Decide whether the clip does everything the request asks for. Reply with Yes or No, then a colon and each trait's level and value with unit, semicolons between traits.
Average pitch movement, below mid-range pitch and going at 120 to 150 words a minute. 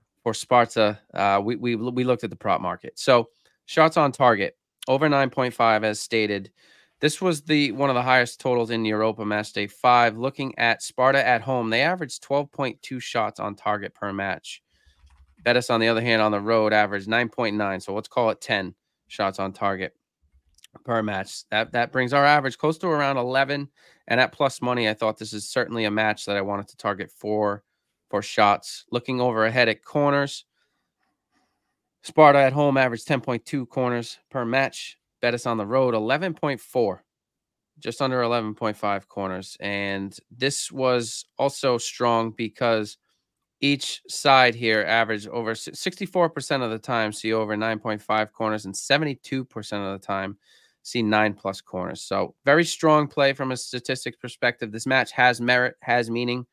No: average, 3.8 semitones; low, 120 Hz; average, 165 wpm